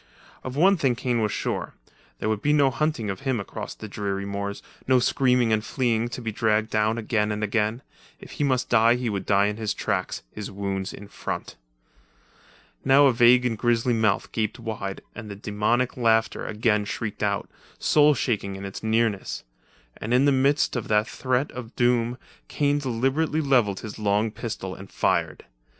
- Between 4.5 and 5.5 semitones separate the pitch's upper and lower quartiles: No, average, 3.2 semitones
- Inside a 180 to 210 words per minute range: Yes, average, 185 wpm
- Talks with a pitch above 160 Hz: No, low, 115 Hz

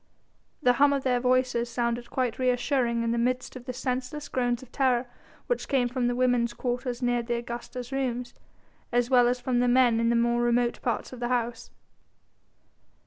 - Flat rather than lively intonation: Yes, narrow, 1.1 semitones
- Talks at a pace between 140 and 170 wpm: No, average, 190 wpm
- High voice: Yes, high, 245 Hz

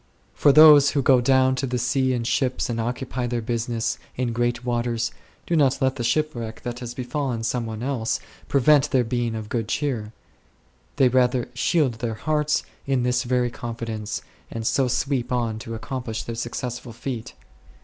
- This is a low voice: Yes, low, 125 Hz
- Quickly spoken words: No, average, 180 wpm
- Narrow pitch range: Yes, narrow, 2.2 semitones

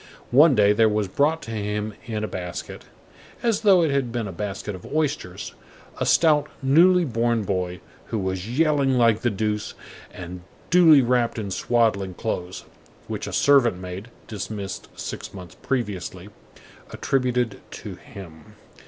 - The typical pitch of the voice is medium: No, low, 110 Hz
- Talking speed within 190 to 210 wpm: No, average, 150 wpm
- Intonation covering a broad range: Yes, wide, 5.8 semitones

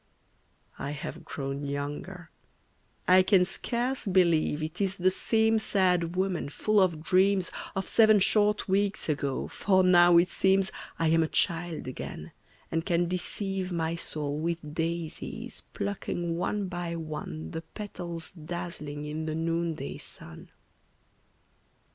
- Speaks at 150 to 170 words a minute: No, slow, 135 wpm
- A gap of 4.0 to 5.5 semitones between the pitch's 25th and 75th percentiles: No, average, 3.2 semitones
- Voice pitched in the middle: Yes, medium, 175 Hz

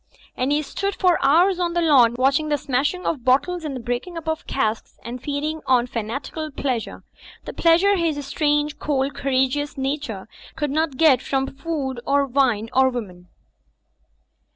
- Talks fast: No, average, 165 wpm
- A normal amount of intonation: Yes, average, 3.6 semitones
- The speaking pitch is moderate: No, very high, 280 Hz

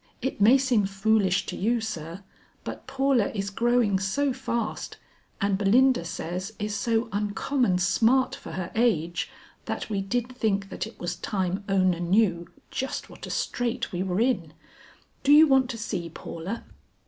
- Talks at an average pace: Yes, average, 160 wpm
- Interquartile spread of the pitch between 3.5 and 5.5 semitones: Yes, average, 4.5 semitones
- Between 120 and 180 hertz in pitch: No, high, 210 Hz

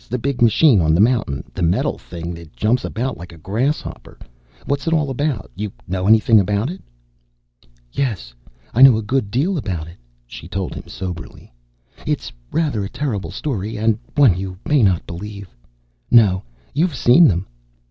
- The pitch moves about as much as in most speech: No, wide, 6.3 semitones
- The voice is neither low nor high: No, low, 105 Hz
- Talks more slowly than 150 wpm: No, average, 170 wpm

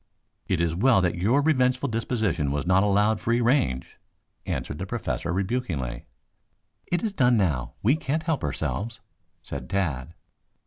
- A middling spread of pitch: No, wide, 7.2 semitones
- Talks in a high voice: No, low, 105 Hz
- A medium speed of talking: Yes, average, 145 wpm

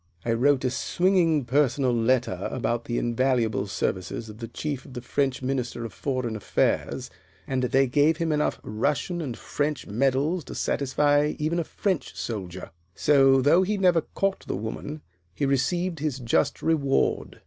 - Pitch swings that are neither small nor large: Yes, average, 4.1 semitones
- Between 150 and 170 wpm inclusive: Yes, average, 160 wpm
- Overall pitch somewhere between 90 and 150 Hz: Yes, low, 135 Hz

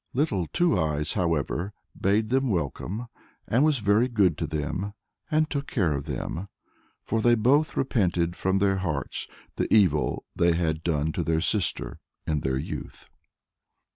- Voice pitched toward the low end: Yes, very low, 95 Hz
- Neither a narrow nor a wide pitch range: No, wide, 6.0 semitones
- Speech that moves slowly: No, average, 155 wpm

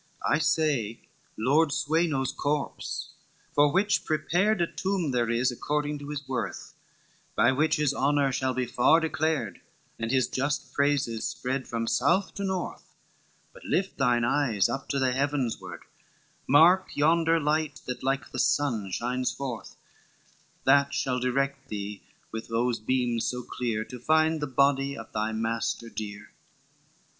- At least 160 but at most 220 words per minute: No, average, 150 wpm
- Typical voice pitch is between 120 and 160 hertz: Yes, low, 135 Hz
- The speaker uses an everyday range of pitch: Yes, average, 3.8 semitones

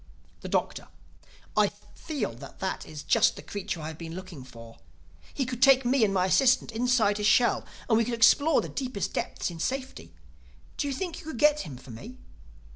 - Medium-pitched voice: No, high, 230 Hz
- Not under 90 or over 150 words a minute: No, average, 200 wpm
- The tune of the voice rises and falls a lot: Yes, wide, 7.2 semitones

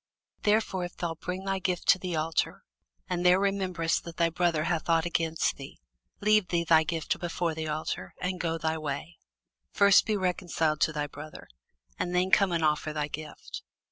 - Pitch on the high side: No, medium, 170 Hz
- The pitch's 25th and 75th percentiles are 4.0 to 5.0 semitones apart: No, narrow, 2.4 semitones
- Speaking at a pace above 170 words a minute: Yes, average, 185 wpm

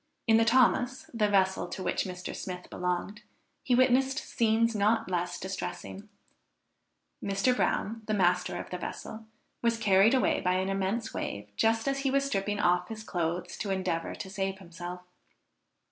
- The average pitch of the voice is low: No, high, 200 Hz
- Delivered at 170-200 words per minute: No, average, 160 wpm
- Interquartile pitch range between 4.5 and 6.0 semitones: No, average, 4.0 semitones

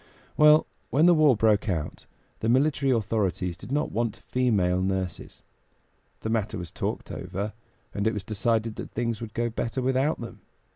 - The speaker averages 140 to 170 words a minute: Yes, average, 165 wpm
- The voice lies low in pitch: Yes, low, 115 Hz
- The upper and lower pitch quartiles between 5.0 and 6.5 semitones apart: No, average, 4.2 semitones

